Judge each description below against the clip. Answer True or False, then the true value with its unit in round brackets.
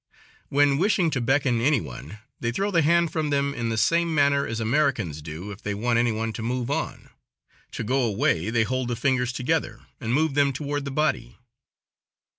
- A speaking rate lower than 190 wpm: False (200 wpm)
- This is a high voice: False (130 Hz)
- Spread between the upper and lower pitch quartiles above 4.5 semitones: False (4.1 semitones)